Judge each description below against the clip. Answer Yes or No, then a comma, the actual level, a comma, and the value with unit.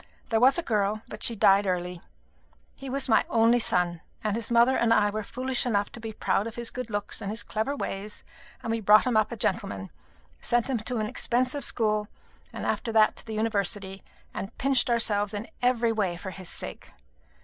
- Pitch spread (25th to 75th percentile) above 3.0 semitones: No, average, 2.7 semitones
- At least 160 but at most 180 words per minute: No, fast, 205 wpm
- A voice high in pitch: Yes, high, 220 Hz